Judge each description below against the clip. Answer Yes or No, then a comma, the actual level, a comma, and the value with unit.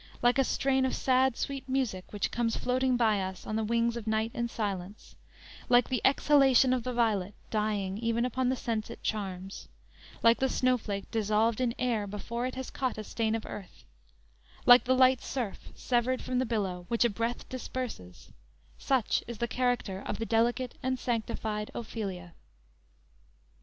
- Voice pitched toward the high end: Yes, high, 235 Hz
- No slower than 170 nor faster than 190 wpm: Yes, average, 175 wpm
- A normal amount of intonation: Yes, average, 3.0 semitones